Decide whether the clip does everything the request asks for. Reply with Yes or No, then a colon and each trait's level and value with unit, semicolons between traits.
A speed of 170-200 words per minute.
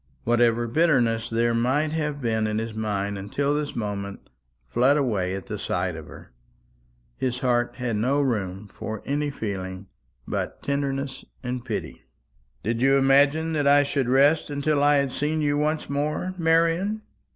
No: average, 155 wpm